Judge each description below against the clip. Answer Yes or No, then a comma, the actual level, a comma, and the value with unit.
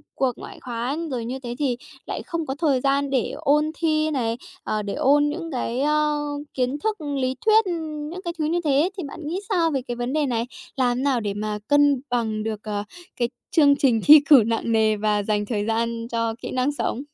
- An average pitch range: Yes, average, 4.5 semitones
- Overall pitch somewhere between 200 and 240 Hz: No, very high, 260 Hz